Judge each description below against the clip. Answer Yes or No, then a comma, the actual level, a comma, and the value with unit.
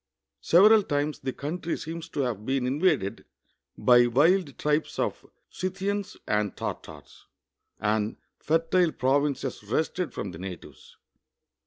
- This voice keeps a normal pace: No, slow, 120 wpm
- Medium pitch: Yes, medium, 145 Hz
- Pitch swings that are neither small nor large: No, wide, 5.8 semitones